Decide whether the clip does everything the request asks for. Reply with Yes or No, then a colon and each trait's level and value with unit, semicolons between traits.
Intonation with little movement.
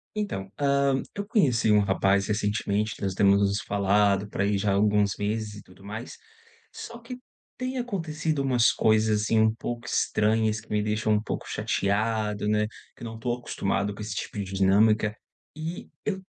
No: average, 3.0 semitones